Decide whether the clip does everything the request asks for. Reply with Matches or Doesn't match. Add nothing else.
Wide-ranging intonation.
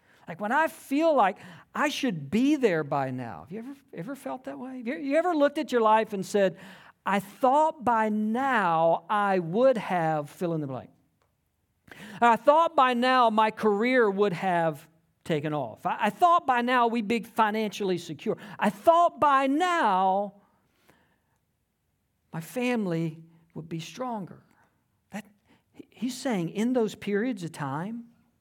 Matches